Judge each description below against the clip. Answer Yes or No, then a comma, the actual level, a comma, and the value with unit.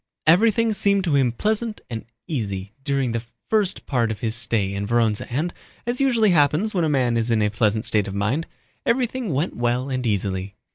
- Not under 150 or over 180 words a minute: No, average, 195 wpm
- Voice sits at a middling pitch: No, low, 130 Hz